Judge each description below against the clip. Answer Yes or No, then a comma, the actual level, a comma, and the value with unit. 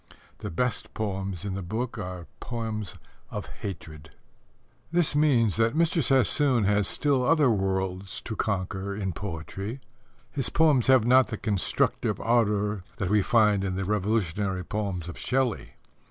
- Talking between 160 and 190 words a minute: No, average, 145 wpm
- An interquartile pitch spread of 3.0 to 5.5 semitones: Yes, average, 4.3 semitones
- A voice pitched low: Yes, low, 105 Hz